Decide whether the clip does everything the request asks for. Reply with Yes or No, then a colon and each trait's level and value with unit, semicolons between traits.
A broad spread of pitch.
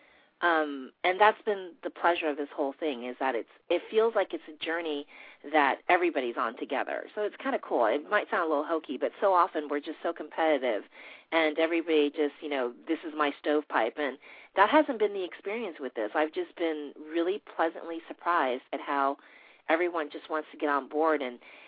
No: average, 2.9 semitones